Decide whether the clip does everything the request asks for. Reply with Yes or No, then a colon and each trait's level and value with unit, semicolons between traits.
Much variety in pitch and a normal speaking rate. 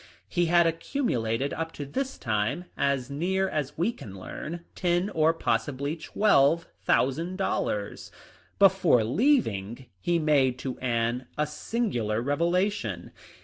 No: wide, 6.0 semitones; slow, 130 wpm